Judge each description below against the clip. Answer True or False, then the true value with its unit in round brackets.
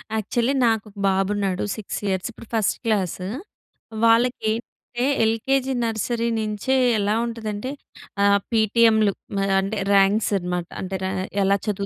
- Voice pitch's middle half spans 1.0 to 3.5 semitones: True (2.7 semitones)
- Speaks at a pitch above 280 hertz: False (215 Hz)